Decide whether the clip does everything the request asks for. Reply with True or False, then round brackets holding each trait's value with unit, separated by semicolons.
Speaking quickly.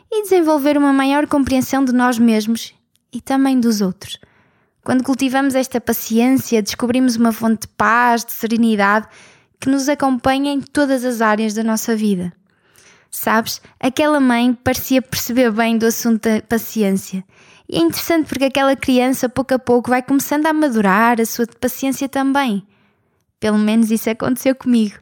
False (155 wpm)